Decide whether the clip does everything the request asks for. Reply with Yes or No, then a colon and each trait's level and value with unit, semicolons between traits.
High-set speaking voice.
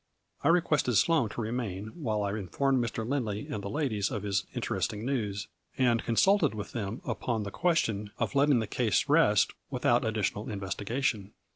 No: low, 115 Hz